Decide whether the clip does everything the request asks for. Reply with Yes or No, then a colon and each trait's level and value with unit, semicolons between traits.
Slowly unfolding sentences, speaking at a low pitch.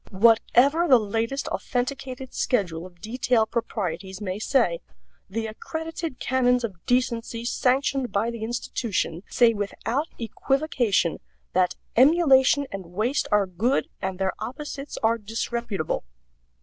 No: slow, 120 wpm; high, 230 Hz